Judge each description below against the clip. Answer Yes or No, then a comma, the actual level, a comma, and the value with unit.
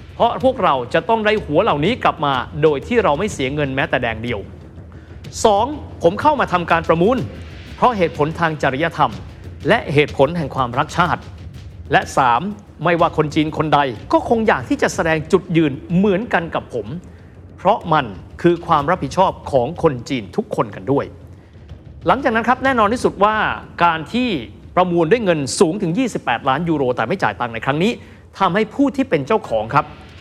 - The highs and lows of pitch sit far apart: Yes, wide, 6.4 semitones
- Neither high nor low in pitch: Yes, medium, 170 Hz